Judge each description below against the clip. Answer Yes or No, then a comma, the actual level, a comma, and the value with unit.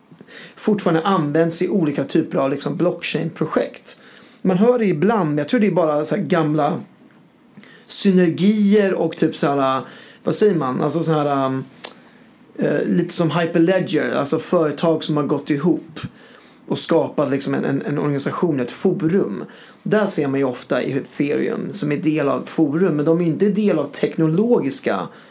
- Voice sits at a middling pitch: Yes, medium, 165 Hz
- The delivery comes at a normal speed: Yes, average, 160 wpm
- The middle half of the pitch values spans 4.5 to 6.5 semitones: Yes, average, 5.1 semitones